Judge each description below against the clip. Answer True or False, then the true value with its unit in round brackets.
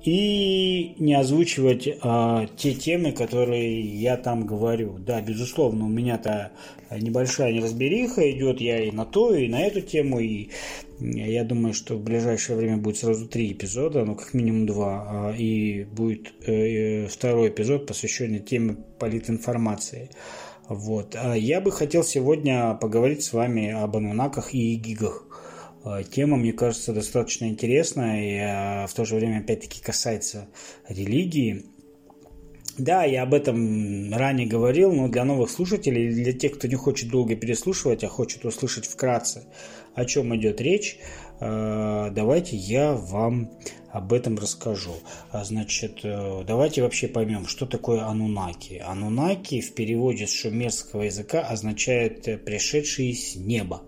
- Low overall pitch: True (115 Hz)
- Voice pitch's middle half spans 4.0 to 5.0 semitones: False (3.2 semitones)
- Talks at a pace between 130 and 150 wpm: True (135 wpm)